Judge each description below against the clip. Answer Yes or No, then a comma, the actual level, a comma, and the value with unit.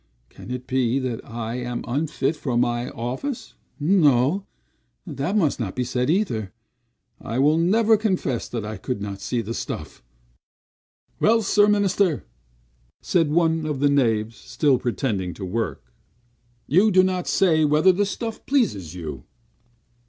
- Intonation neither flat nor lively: No, wide, 7.7 semitones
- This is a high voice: No, low, 135 Hz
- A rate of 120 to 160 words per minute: Yes, average, 145 wpm